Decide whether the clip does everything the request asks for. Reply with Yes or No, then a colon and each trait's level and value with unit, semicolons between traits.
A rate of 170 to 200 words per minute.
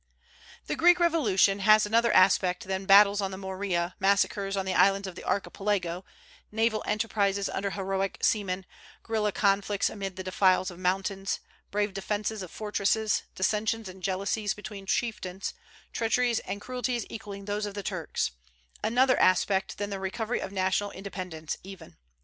No: average, 150 wpm